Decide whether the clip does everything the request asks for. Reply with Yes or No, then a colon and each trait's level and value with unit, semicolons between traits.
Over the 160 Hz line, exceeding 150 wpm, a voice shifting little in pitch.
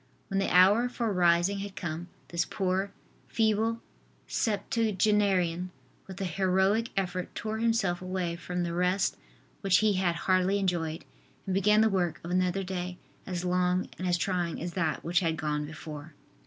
Yes: medium, 185 Hz; average, 160 wpm; narrow, 2.3 semitones